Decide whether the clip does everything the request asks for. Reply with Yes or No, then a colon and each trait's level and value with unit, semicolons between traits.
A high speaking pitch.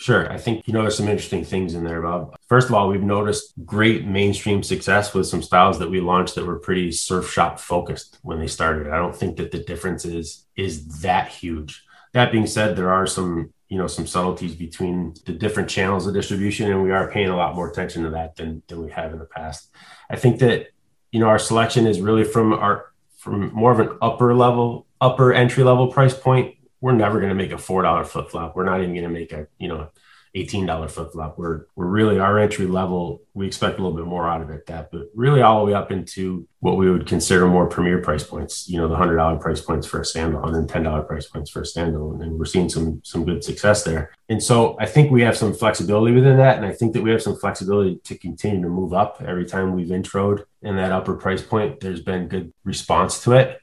No: very low, 95 Hz